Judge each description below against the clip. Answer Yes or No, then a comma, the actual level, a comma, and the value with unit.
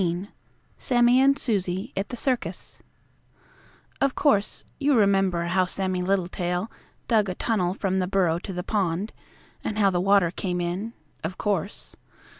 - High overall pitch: Yes, high, 195 Hz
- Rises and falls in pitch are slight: No, average, 3.4 semitones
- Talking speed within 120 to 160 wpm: Yes, average, 150 wpm